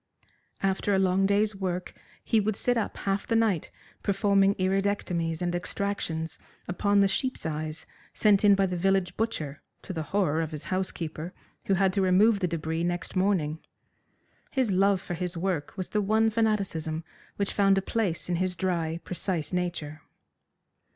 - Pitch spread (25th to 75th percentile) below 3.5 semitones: Yes, average, 2.9 semitones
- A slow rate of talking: No, average, 165 wpm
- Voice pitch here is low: No, high, 190 Hz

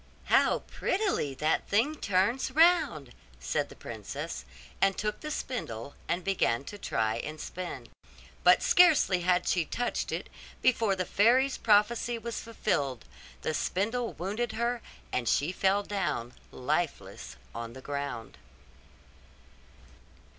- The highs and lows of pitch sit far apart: Yes, wide, 8.6 semitones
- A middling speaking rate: No, slow, 130 wpm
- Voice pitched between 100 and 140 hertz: No, high, 195 Hz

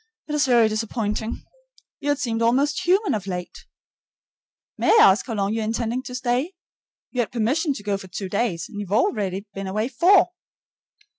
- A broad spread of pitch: No, average, 4.4 semitones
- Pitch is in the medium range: No, high, 230 Hz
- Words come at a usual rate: Yes, average, 180 wpm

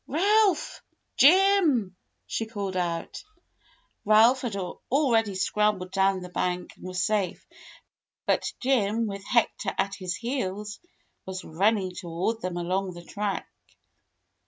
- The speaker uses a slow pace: Yes, slow, 125 wpm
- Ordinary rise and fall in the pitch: Yes, average, 4.1 semitones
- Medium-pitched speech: No, high, 200 Hz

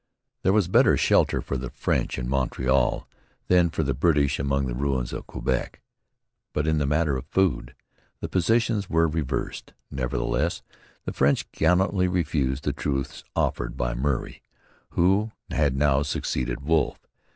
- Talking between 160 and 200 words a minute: No, average, 150 wpm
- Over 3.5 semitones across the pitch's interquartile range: Yes, average, 4.4 semitones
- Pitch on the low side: Yes, very low, 70 Hz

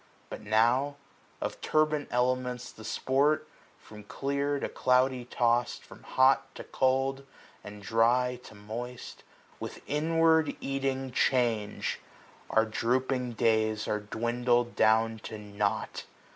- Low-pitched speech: Yes, low, 125 Hz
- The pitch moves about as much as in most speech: Yes, average, 3.2 semitones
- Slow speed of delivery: Yes, slow, 120 wpm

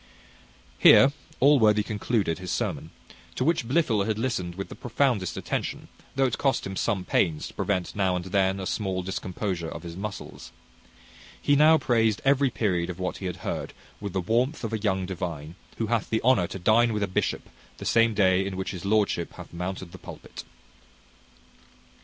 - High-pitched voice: No, low, 100 Hz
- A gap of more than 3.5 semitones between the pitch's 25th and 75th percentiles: Yes, average, 3.9 semitones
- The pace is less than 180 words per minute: No, average, 185 wpm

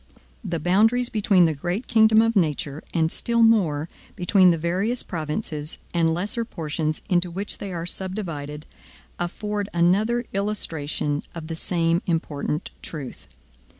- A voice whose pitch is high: No, medium, 175 Hz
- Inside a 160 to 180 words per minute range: No, slow, 135 wpm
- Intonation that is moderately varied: Yes, average, 4.6 semitones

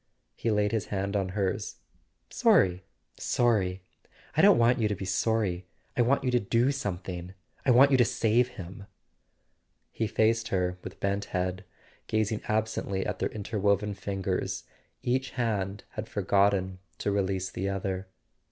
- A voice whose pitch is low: Yes, low, 100 Hz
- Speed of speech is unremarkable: Yes, average, 150 wpm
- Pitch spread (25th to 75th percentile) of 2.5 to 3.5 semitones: Yes, average, 2.9 semitones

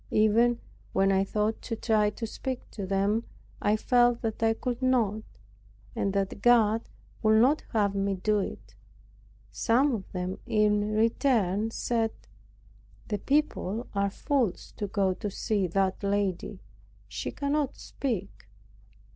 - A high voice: Yes, high, 215 Hz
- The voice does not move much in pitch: No, average, 3.0 semitones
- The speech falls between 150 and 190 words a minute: No, average, 140 wpm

